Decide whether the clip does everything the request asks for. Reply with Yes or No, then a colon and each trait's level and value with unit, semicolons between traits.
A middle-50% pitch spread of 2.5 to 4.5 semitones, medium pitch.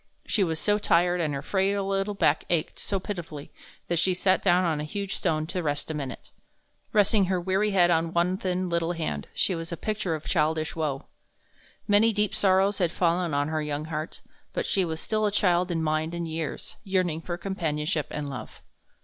Yes: average, 3.4 semitones; medium, 175 Hz